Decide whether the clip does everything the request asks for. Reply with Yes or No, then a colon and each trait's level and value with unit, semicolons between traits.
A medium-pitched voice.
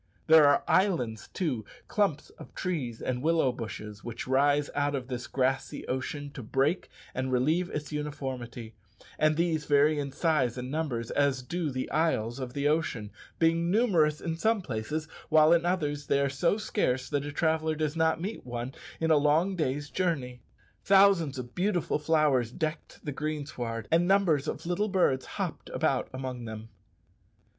Yes: medium, 145 Hz